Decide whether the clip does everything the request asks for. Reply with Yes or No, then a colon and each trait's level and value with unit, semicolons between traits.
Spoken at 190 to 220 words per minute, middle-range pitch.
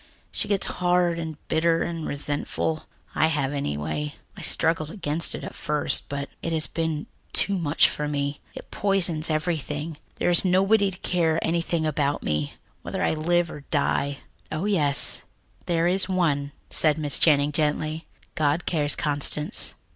No: average, 155 wpm; medium, 155 Hz